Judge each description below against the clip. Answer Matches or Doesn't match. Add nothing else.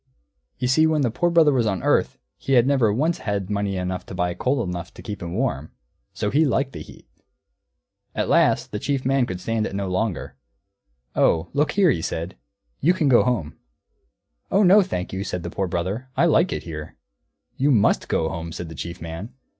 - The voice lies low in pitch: Matches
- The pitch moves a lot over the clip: Matches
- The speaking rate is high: Matches